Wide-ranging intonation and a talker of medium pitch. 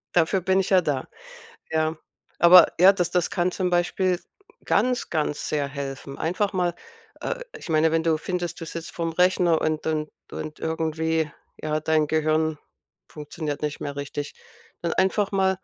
No: average, 2.7 semitones; medium, 160 Hz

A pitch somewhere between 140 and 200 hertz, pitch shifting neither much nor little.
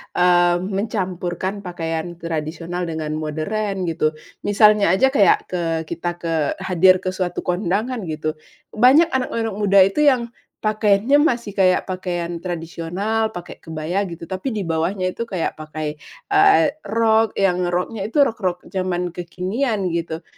Yes: medium, 185 Hz; average, 3.9 semitones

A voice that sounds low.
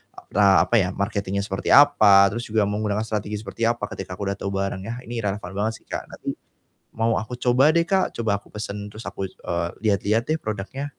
Yes: low, 105 Hz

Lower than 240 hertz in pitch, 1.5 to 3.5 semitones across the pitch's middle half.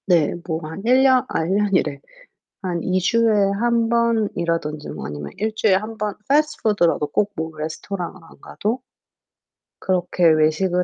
No: medium, 185 Hz; wide, 5.4 semitones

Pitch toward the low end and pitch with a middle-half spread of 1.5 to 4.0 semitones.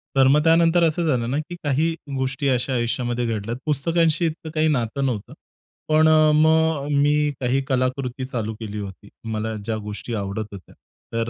No: low, 130 Hz; average, 5.1 semitones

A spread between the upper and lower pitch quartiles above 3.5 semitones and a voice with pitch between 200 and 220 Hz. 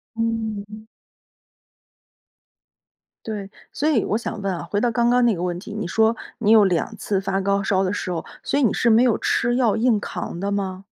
No: average, 2.8 semitones; high, 210 Hz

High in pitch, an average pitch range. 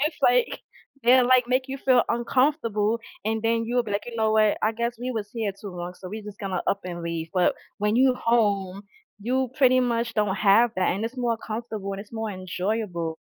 Yes: high, 220 Hz; average, 3.4 semitones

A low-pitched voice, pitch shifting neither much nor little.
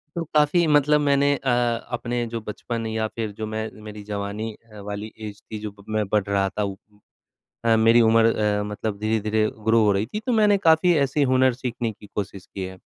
Yes: low, 110 Hz; average, 3.6 semitones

